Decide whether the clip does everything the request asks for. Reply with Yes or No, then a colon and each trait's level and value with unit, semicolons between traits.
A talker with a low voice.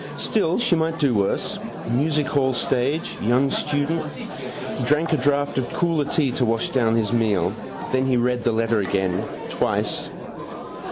Yes: low, 130 Hz